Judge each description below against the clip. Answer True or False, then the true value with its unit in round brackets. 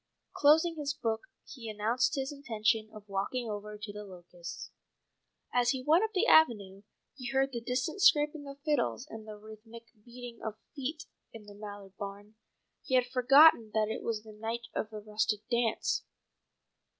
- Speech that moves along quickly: False (170 wpm)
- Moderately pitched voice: False (230 Hz)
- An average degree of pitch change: True (4.1 semitones)